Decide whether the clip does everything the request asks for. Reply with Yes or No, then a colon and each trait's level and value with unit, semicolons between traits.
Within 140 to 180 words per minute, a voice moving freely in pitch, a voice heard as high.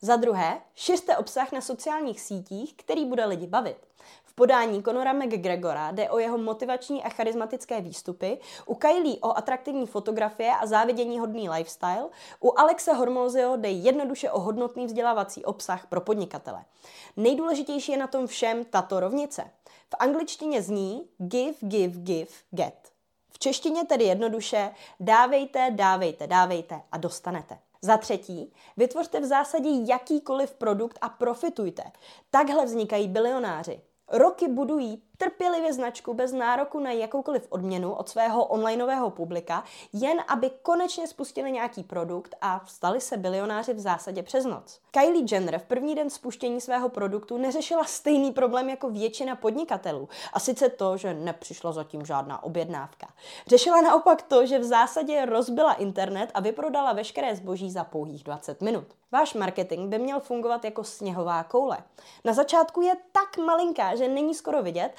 Yes: average, 145 wpm; wide, 6.1 semitones; high, 240 Hz